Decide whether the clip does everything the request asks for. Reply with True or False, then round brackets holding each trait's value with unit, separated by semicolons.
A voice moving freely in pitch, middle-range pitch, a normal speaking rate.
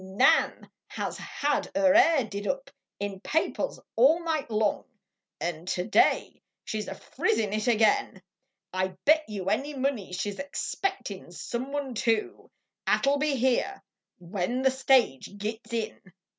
False (5.7 semitones; 235 Hz; 145 wpm)